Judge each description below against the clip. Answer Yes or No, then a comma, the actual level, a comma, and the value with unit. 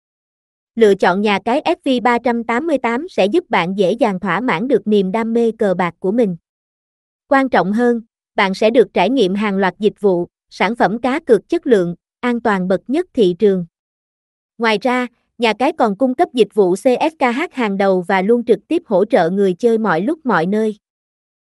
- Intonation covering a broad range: No, average, 3.8 semitones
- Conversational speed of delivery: Yes, average, 190 wpm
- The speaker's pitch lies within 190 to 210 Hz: No, high, 225 Hz